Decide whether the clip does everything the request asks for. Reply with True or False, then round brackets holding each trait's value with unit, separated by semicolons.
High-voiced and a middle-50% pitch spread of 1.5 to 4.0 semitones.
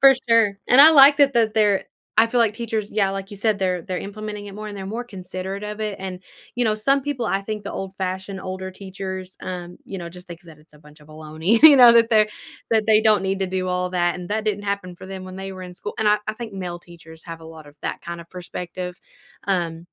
True (195 Hz; 3.1 semitones)